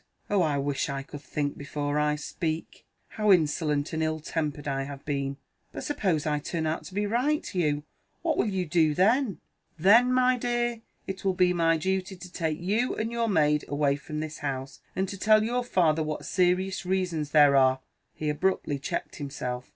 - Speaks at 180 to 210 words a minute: Yes, average, 190 wpm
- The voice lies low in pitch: No, medium, 160 Hz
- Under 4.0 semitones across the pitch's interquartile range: No, average, 4.6 semitones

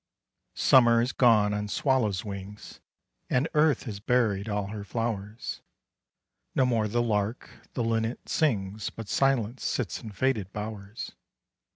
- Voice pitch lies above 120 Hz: No, low, 110 Hz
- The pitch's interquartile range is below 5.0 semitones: Yes, average, 3.0 semitones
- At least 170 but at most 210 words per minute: No, slow, 135 wpm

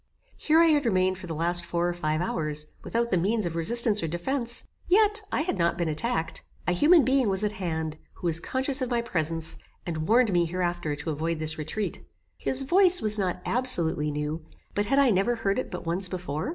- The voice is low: No, medium, 185 Hz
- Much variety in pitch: Yes, wide, 6.5 semitones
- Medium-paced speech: No, fast, 215 wpm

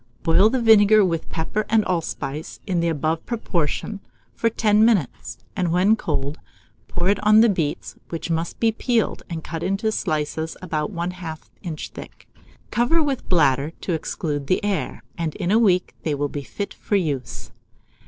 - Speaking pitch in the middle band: Yes, medium, 175 Hz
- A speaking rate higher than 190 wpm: No, average, 170 wpm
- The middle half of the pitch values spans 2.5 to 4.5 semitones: No, average, 5.1 semitones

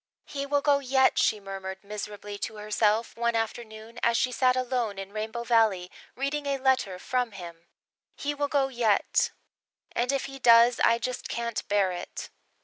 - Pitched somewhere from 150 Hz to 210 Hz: No, high, 230 Hz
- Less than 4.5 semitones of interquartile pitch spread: Yes, average, 3.8 semitones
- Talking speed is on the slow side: No, average, 170 wpm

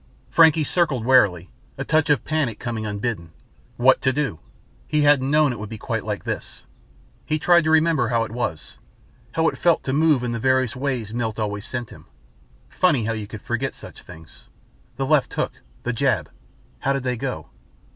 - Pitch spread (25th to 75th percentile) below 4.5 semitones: No, average, 5.0 semitones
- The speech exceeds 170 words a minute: Yes, average, 190 wpm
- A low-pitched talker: Yes, low, 130 Hz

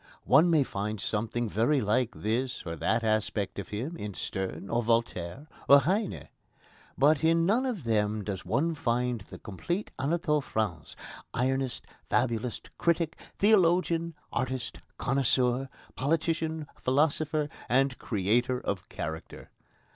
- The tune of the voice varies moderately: No, wide, 6.3 semitones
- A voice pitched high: No, low, 130 Hz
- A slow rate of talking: Yes, slow, 125 wpm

